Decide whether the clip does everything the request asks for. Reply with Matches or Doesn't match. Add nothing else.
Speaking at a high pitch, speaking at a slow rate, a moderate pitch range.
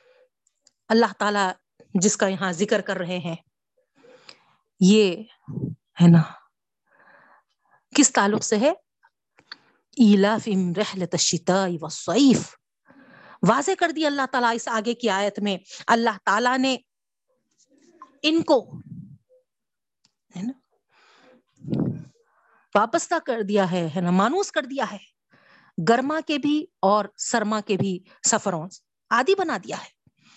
Doesn't match